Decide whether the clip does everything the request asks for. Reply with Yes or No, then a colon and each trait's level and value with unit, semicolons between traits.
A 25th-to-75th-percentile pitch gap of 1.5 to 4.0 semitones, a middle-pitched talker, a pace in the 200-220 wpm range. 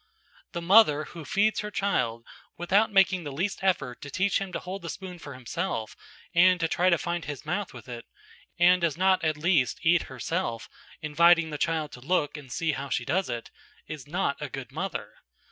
No: average, 4.5 semitones; medium, 170 Hz; fast, 205 wpm